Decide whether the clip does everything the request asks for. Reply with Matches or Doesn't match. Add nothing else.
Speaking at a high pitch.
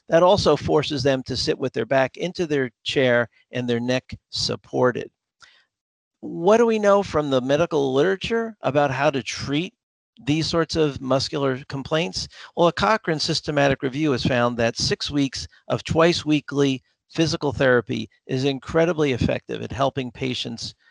Doesn't match